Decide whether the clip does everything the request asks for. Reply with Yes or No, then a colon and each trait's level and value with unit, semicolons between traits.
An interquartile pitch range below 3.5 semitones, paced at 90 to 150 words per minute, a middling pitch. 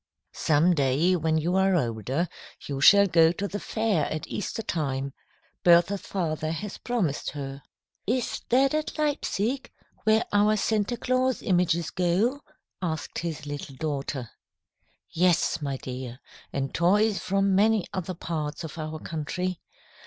No: average, 5.3 semitones; average, 140 wpm; medium, 175 Hz